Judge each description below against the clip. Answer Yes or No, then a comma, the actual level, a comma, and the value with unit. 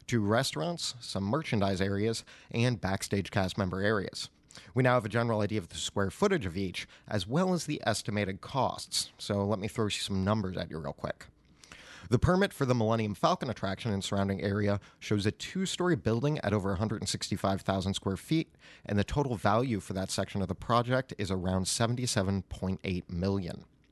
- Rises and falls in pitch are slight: No, average, 3.5 semitones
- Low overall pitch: Yes, low, 105 Hz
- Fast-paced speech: No, average, 180 wpm